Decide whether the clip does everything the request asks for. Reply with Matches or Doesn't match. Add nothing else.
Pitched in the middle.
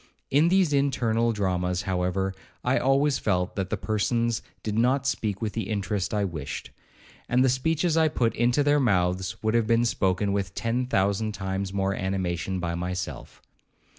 Doesn't match